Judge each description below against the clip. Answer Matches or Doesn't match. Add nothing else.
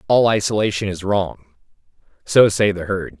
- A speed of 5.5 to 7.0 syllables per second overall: Doesn't match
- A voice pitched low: Matches